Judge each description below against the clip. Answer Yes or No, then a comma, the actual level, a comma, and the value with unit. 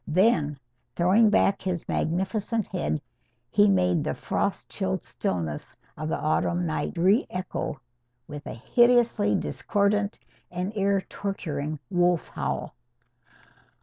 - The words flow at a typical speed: No, slow, 115 wpm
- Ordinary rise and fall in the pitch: Yes, average, 5.0 semitones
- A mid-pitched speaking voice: Yes, medium, 180 Hz